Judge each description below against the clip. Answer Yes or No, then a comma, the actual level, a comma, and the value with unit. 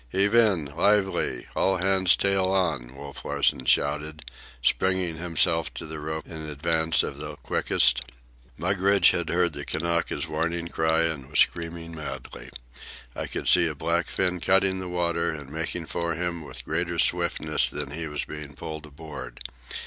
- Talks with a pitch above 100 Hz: No, very low, 85 Hz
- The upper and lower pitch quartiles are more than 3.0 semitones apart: No, average, 2.7 semitones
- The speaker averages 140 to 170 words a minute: Yes, average, 160 wpm